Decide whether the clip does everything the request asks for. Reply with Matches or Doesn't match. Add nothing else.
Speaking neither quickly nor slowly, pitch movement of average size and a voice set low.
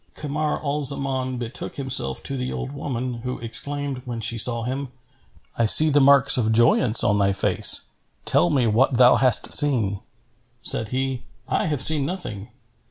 Matches